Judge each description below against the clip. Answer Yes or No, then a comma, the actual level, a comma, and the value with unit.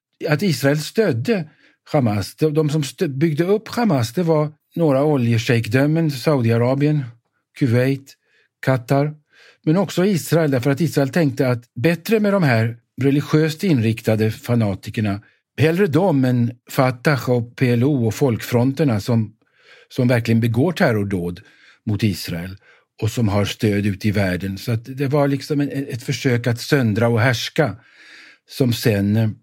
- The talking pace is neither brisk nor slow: Yes, average, 135 wpm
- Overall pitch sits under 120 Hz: No, low, 135 Hz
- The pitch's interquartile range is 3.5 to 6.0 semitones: Yes, average, 4.7 semitones